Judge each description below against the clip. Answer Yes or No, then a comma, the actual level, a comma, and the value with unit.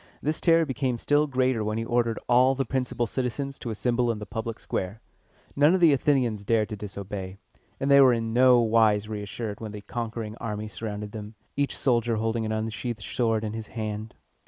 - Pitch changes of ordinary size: Yes, average, 3.0 semitones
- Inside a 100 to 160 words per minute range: No, average, 195 wpm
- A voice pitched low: Yes, low, 115 Hz